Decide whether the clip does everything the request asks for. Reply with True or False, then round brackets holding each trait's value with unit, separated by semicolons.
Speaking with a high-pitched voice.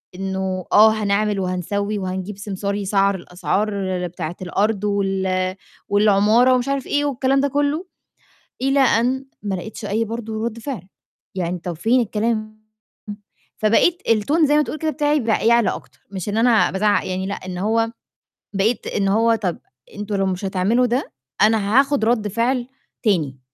True (210 Hz)